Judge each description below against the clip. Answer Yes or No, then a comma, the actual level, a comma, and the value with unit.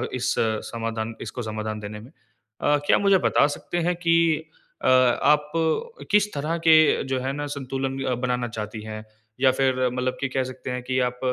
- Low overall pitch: Yes, low, 130 Hz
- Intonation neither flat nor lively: Yes, average, 4.1 semitones